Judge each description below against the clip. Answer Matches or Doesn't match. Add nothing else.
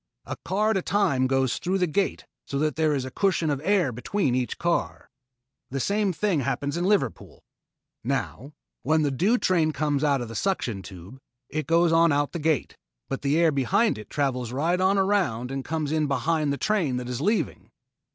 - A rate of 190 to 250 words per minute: Matches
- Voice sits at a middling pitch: Matches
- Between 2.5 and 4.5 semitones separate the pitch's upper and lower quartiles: Doesn't match